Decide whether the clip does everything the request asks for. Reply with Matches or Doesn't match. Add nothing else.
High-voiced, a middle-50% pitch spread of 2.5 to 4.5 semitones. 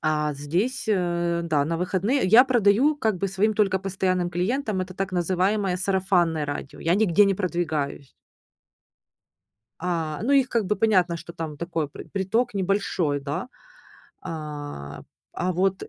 Doesn't match